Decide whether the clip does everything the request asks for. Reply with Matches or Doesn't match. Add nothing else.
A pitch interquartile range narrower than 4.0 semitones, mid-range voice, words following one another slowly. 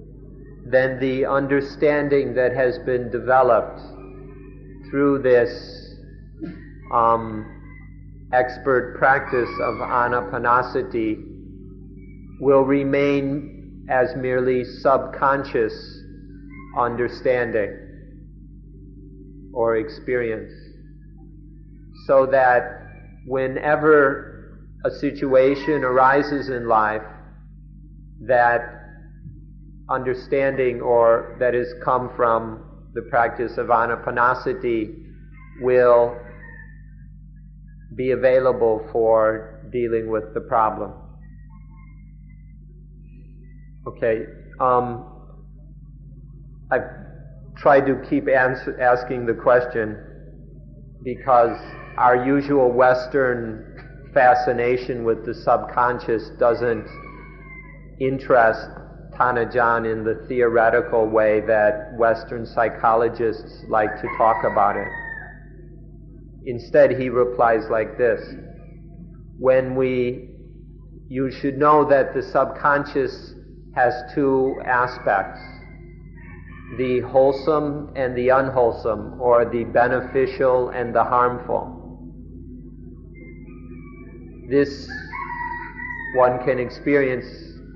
Doesn't match